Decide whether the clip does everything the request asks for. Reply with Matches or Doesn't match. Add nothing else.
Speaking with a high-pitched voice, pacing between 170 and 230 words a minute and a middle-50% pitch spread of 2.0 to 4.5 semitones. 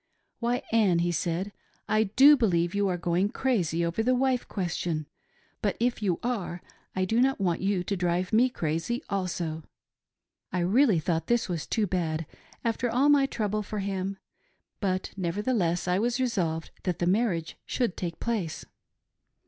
Doesn't match